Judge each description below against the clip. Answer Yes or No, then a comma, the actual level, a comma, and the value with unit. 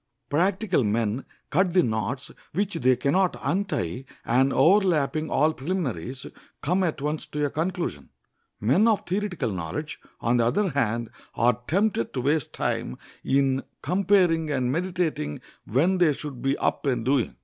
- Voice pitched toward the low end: No, medium, 145 Hz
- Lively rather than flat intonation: Yes, wide, 6.5 semitones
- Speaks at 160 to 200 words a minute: No, average, 150 wpm